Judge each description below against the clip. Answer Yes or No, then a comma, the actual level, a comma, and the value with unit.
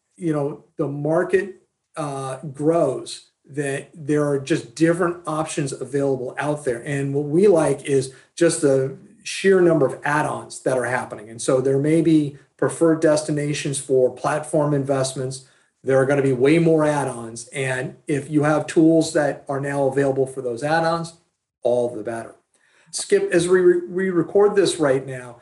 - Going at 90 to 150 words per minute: No, average, 170 wpm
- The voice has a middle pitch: Yes, medium, 145 Hz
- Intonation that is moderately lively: Yes, average, 3.4 semitones